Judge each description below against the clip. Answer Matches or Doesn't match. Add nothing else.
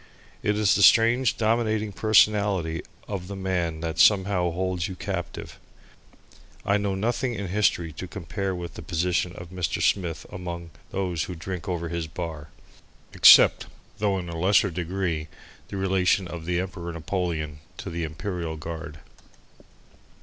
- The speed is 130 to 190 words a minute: Matches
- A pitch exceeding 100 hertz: Doesn't match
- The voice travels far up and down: Doesn't match